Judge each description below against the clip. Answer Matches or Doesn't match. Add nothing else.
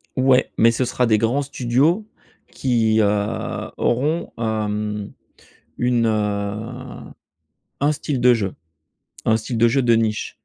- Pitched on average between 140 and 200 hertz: Doesn't match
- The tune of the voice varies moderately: Matches